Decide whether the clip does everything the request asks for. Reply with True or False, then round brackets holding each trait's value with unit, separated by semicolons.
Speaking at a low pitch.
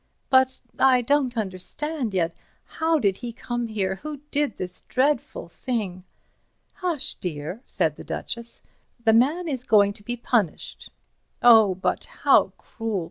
False (235 Hz)